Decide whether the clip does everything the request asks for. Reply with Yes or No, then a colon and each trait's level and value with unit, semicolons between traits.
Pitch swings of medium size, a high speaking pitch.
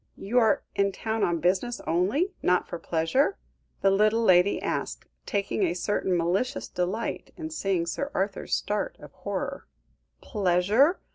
Yes: average, 4.3 semitones; high, 200 Hz